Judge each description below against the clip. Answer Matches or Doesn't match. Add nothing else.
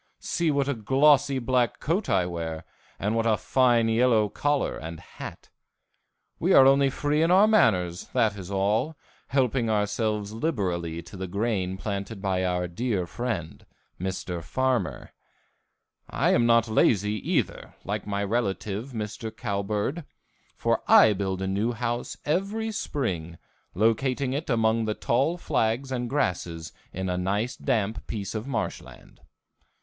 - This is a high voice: Doesn't match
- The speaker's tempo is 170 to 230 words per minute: Doesn't match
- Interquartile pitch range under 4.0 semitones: Doesn't match